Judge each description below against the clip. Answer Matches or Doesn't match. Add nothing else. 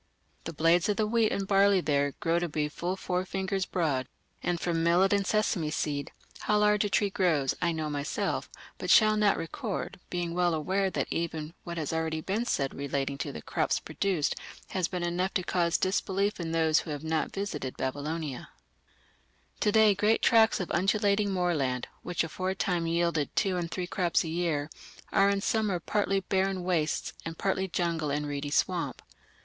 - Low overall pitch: Doesn't match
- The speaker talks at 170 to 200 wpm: Matches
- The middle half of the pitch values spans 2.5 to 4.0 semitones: Matches